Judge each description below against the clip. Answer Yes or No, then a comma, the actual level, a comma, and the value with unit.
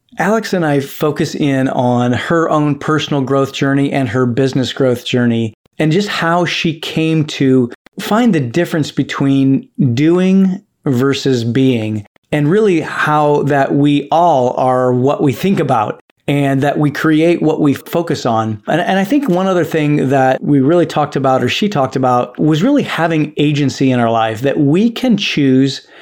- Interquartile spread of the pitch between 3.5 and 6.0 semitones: Yes, average, 3.8 semitones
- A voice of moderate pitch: Yes, medium, 145 Hz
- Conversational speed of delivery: Yes, average, 175 wpm